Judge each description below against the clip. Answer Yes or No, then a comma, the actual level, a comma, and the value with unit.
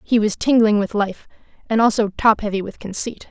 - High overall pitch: Yes, high, 215 Hz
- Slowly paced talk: No, average, 200 wpm